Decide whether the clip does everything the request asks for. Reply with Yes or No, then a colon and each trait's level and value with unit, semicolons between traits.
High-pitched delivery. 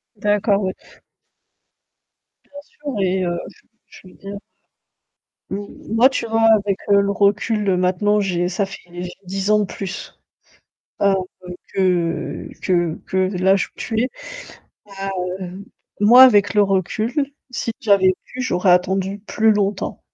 Yes: high, 200 Hz